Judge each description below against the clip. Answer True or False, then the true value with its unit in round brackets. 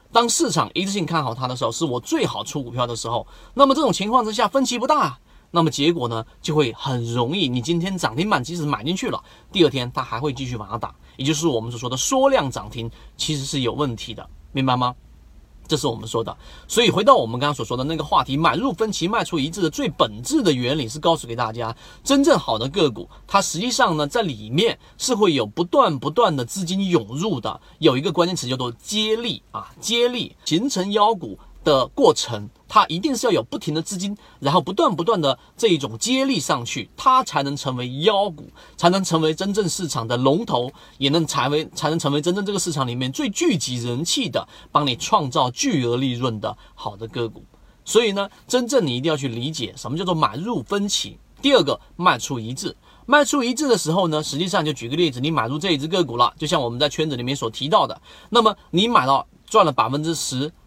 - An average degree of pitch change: False (7.5 semitones)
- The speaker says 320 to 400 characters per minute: True (330 characters per minute)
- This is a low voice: False (155 Hz)